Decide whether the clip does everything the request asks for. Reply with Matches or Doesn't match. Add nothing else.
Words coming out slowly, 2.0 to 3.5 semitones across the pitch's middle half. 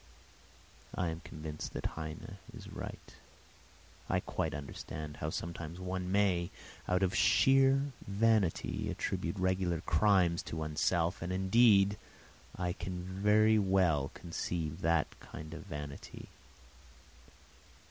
Matches